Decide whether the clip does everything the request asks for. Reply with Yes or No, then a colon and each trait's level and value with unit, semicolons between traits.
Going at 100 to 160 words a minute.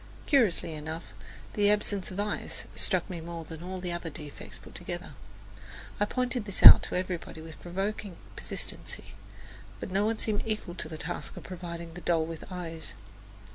No: average, 175 wpm